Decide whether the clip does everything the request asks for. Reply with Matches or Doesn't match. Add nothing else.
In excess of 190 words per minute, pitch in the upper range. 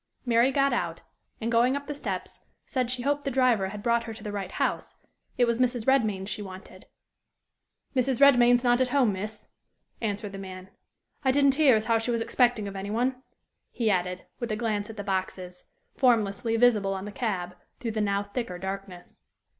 Matches